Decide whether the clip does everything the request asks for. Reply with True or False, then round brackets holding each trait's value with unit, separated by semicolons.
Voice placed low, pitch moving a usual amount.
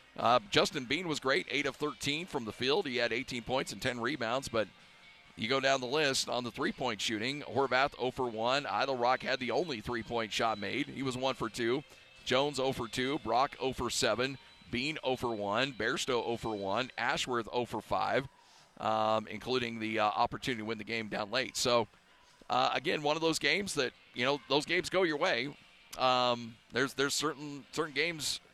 True (130 Hz; 3.0 semitones)